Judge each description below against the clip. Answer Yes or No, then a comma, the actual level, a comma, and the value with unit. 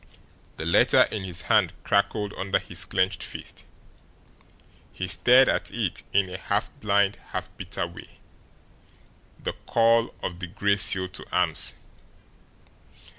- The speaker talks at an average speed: No, slow, 130 wpm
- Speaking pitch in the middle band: No, very low, 95 Hz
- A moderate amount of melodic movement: No, narrow, 2.0 semitones